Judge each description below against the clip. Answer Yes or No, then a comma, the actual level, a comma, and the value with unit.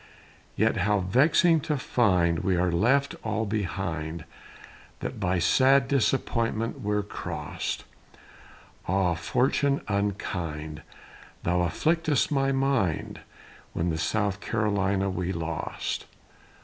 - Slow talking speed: Yes, slow, 105 wpm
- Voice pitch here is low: Yes, low, 100 Hz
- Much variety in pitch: Yes, wide, 6.4 semitones